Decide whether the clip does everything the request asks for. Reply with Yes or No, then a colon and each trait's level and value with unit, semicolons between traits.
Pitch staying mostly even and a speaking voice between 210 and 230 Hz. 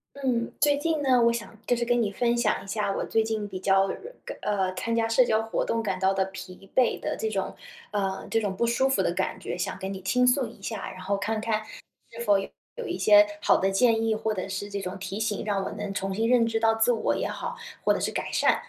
No: average, 3.2 semitones; high, 220 Hz